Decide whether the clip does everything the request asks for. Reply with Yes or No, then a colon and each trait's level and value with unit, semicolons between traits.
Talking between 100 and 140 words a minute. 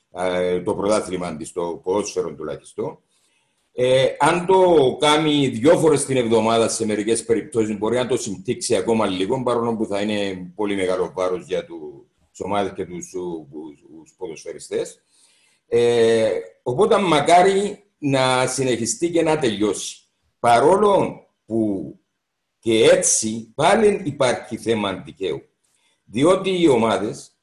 Yes: average, 120 wpm